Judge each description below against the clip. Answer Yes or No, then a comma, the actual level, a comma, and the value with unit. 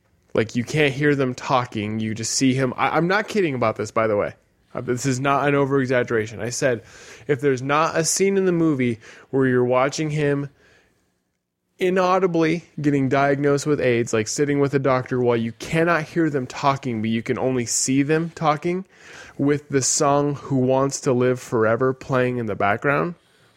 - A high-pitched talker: No, low, 135 Hz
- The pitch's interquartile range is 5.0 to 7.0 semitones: No, average, 3.3 semitones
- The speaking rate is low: No, average, 190 wpm